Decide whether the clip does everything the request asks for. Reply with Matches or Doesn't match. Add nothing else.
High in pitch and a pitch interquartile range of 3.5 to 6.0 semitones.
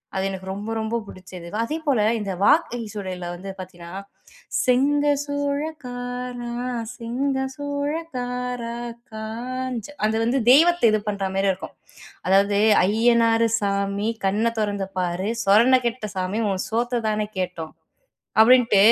Matches